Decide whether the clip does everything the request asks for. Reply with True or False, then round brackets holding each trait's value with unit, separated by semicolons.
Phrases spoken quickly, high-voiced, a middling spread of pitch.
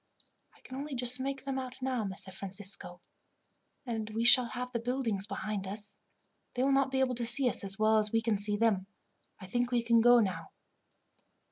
True (210 wpm; 235 Hz; 3.6 semitones)